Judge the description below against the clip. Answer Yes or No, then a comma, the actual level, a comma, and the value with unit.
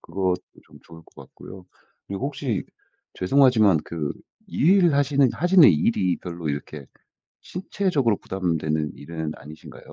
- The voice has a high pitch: No, very low, 95 Hz